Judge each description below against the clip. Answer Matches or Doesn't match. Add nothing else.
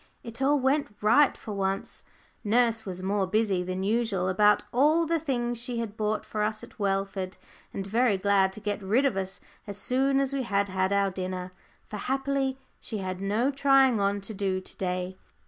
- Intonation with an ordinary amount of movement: Matches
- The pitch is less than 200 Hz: Doesn't match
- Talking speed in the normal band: Matches